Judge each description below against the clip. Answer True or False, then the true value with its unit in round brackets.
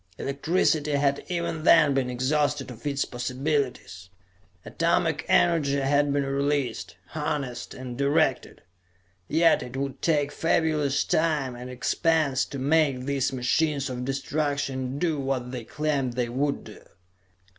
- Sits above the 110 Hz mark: True (140 Hz)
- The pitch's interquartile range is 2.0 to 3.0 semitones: True (2.7 semitones)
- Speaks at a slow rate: True (130 wpm)